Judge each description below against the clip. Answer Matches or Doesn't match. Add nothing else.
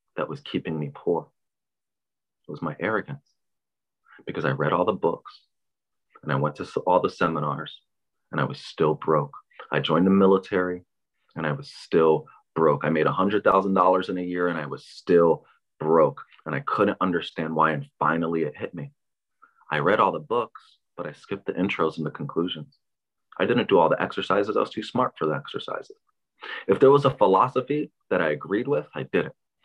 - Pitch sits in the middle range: Doesn't match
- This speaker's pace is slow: Doesn't match